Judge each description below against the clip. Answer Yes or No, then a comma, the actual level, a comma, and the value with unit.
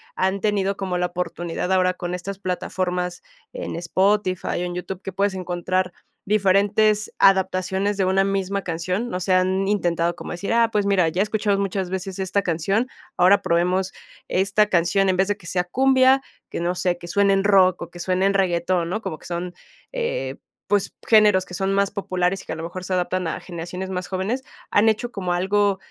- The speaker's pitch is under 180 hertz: No, high, 190 Hz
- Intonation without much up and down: Yes, narrow, 1.9 semitones